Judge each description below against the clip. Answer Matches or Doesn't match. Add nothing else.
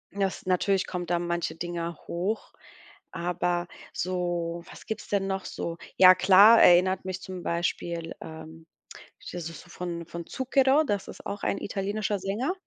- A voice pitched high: Doesn't match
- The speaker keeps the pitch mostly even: Matches